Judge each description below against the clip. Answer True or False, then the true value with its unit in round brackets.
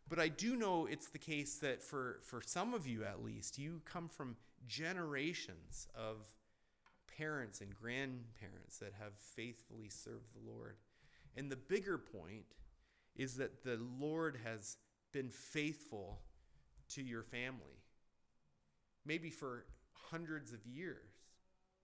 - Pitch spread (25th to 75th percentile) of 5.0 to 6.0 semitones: True (5.6 semitones)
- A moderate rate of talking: False (130 wpm)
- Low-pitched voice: True (125 Hz)